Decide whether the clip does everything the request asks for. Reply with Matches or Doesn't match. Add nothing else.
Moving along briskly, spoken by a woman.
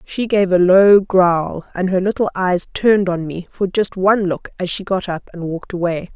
Matches